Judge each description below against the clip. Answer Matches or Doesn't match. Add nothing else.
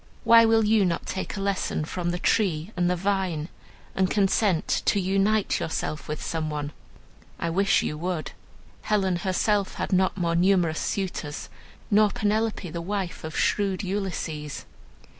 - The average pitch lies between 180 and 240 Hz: Matches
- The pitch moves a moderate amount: Matches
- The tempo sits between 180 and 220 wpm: Doesn't match